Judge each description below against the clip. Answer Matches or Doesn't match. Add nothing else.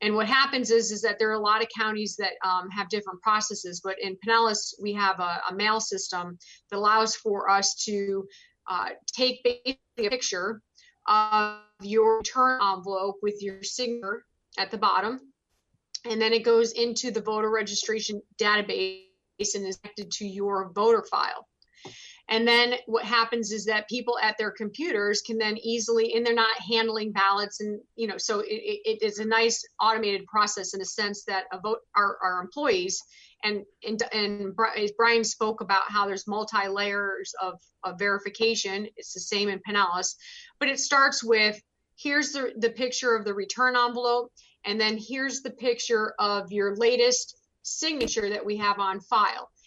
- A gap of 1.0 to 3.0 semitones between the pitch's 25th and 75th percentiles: Matches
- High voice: Matches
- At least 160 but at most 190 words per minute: Matches